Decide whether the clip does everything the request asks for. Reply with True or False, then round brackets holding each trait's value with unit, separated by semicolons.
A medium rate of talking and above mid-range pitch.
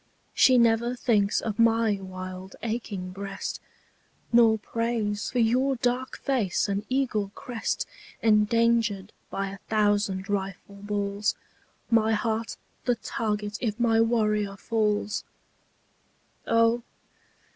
False (110 wpm; 215 Hz)